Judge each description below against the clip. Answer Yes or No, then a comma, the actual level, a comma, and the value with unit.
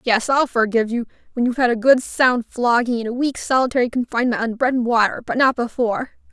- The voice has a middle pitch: No, high, 240 Hz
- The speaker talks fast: Yes, fast, 220 wpm